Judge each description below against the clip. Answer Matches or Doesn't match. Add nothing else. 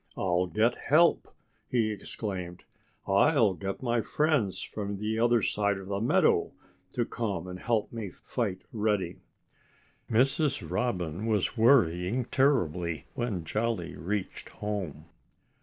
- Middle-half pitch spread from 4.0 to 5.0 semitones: Matches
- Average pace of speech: Doesn't match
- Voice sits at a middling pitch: Doesn't match